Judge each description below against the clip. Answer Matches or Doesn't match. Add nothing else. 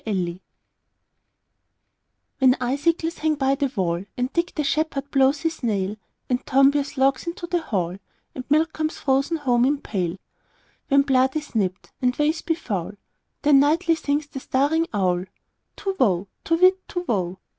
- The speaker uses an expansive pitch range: Matches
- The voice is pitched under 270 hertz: Doesn't match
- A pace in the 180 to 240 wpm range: Doesn't match